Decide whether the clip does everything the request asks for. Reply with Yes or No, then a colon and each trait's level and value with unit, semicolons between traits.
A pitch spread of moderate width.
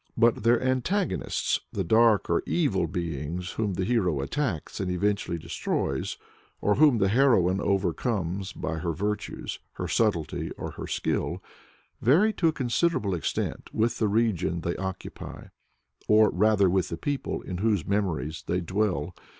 Yes: average, 4.8 semitones